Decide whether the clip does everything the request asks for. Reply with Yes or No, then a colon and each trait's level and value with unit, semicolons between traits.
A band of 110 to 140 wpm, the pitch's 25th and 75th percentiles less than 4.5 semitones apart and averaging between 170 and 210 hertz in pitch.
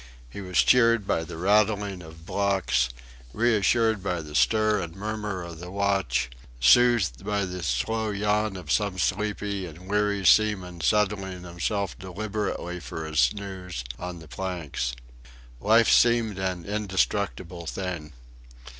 No: slow, 135 wpm; average, 3.2 semitones; very low, 95 Hz